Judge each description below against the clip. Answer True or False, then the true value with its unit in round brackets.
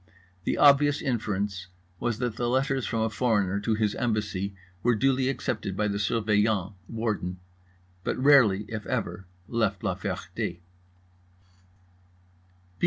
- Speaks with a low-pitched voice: True (110 Hz)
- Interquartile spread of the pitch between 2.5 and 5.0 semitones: True (3.4 semitones)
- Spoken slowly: True (125 wpm)